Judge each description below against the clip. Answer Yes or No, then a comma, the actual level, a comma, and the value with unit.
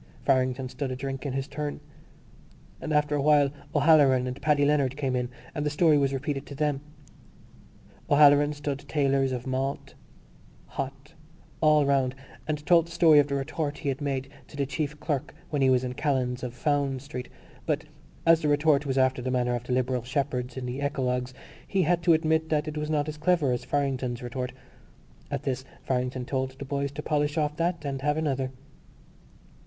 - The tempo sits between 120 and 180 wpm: No, average, 190 wpm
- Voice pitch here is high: No, medium, 140 Hz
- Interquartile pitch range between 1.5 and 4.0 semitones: Yes, narrow, 2.4 semitones